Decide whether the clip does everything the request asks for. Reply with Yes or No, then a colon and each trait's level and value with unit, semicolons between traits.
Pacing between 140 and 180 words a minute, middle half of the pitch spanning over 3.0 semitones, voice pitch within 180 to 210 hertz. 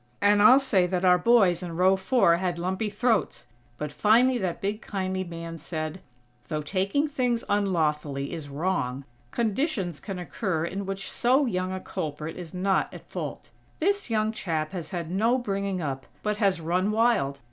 Yes: average, 170 wpm; average, 4.2 semitones; high, 190 Hz